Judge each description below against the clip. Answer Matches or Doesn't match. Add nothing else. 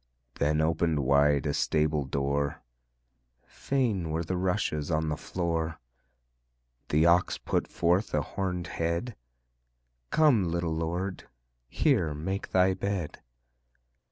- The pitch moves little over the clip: Doesn't match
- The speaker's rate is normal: Doesn't match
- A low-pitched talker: Matches